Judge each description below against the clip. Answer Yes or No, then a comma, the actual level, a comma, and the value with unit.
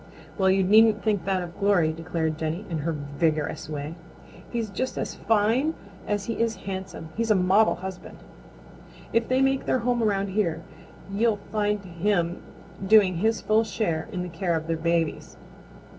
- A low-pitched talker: No, high, 195 Hz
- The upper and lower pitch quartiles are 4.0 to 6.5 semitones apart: Yes, average, 4.5 semitones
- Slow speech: No, average, 170 wpm